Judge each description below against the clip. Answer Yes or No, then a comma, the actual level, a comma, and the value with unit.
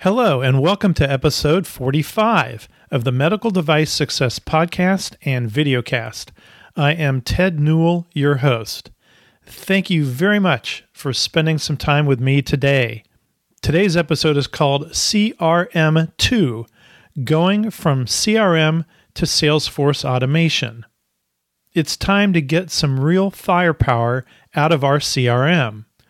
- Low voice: No, medium, 150 Hz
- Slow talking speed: Yes, slow, 125 wpm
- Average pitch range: Yes, average, 4.6 semitones